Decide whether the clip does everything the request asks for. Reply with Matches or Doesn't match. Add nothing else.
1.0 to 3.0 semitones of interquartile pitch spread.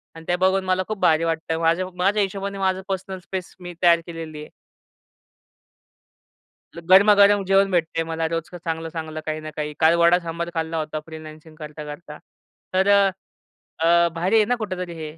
Matches